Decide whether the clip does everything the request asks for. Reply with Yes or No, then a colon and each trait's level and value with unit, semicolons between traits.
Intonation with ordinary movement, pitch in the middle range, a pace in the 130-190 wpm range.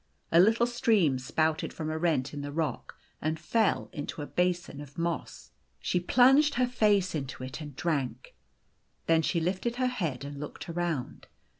No: wide, 6.0 semitones; medium, 165 Hz; average, 170 wpm